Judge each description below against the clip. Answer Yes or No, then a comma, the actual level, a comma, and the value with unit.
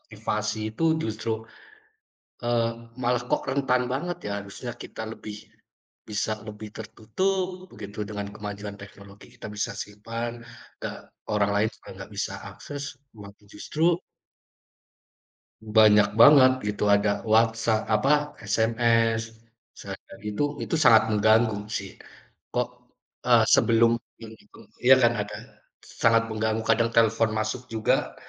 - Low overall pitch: Yes, low, 110 Hz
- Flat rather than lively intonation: Yes, narrow, 2.1 semitones